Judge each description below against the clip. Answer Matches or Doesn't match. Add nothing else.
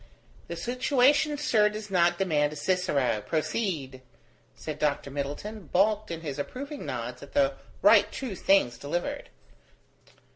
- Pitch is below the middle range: Doesn't match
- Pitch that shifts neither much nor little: Doesn't match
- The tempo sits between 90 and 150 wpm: Matches